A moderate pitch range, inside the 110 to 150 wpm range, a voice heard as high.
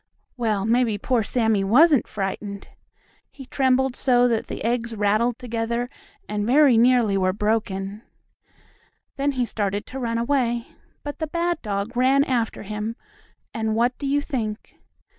Yes: average, 3.4 semitones; average, 145 wpm; high, 235 Hz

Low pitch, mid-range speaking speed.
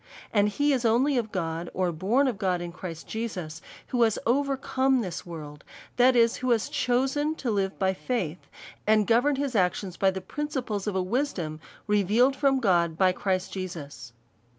No: high, 210 Hz; average, 175 wpm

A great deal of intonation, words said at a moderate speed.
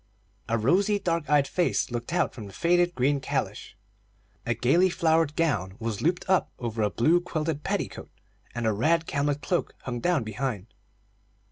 Yes: wide, 6.4 semitones; average, 165 wpm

